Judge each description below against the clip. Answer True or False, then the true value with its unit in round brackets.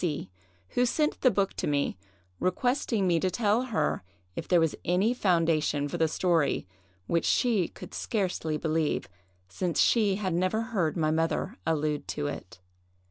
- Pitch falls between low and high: True (175 Hz)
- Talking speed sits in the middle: True (160 wpm)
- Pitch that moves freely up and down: False (4.9 semitones)